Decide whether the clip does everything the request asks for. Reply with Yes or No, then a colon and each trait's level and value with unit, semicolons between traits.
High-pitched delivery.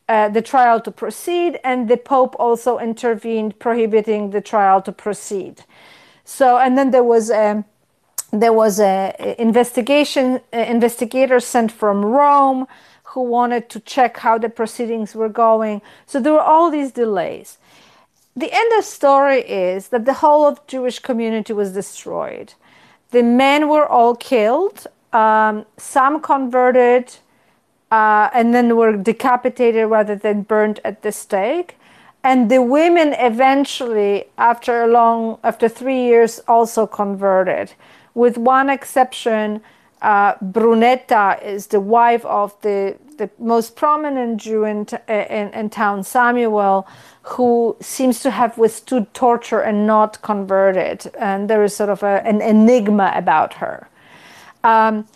Yes: high, 230 Hz